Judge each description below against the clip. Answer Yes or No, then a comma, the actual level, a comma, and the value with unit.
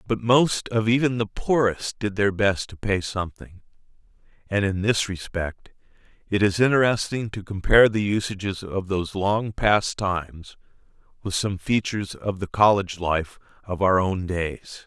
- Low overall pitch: Yes, low, 100 Hz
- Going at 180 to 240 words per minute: No, average, 155 wpm